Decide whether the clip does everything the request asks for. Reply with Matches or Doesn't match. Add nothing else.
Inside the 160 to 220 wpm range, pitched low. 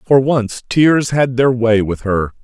Matches